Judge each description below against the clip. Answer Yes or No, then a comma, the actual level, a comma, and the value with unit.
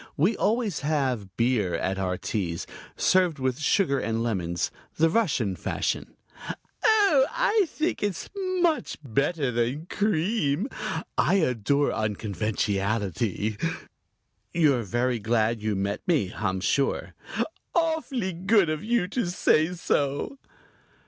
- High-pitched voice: No, medium, 140 Hz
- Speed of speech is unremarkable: No, slow, 115 wpm